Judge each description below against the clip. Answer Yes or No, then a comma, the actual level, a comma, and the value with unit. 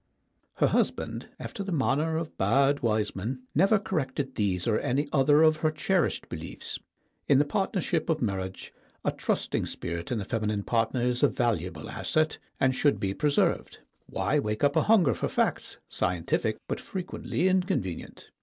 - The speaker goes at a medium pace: Yes, average, 165 wpm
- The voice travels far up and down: Yes, wide, 6.6 semitones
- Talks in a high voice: No, low, 135 Hz